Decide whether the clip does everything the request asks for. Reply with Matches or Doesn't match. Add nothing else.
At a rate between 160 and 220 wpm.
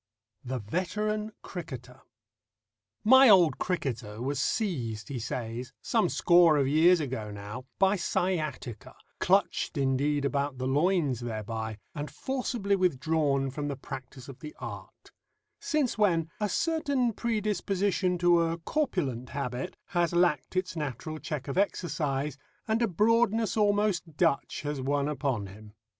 Doesn't match